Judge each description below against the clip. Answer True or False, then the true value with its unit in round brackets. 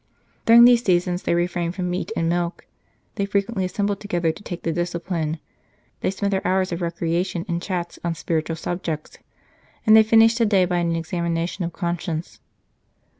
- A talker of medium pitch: True (175 Hz)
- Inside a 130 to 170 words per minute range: False (190 wpm)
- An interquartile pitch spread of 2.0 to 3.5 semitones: True (2.5 semitones)